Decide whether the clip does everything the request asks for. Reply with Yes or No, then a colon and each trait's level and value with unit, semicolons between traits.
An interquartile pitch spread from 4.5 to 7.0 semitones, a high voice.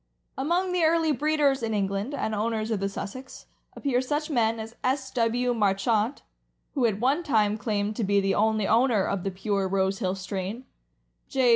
Yes: average, 4.8 semitones; high, 225 Hz